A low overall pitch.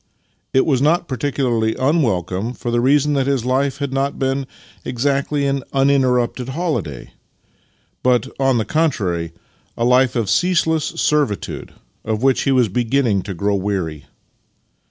Yes: low, 130 Hz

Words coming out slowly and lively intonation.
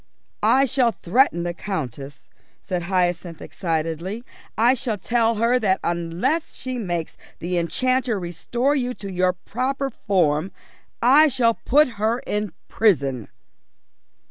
Yes: slow, 125 wpm; wide, 6.3 semitones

